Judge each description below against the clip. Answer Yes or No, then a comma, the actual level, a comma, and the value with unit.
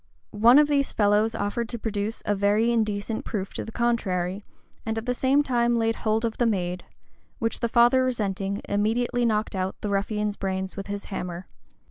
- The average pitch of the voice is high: Yes, high, 215 Hz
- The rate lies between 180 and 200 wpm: Yes, average, 185 wpm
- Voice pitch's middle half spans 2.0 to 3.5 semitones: Yes, average, 2.8 semitones